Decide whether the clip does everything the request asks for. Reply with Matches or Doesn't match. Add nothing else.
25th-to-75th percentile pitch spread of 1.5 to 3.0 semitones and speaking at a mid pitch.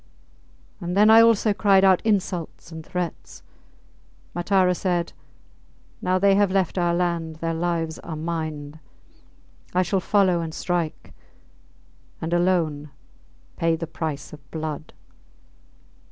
Matches